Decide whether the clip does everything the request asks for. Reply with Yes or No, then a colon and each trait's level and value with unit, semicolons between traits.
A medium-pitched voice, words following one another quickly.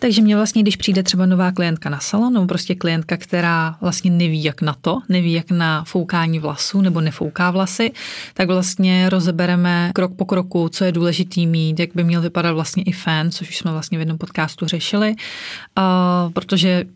Yes: medium, 180 Hz; fast, 185 wpm